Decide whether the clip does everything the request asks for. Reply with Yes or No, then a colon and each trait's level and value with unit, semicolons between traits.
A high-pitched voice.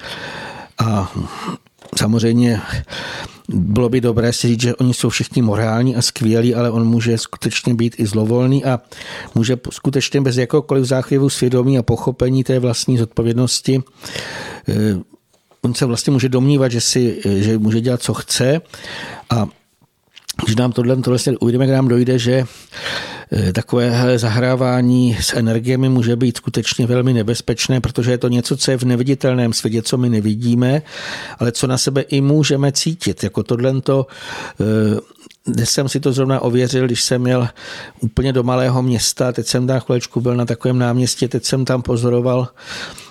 No: low, 125 Hz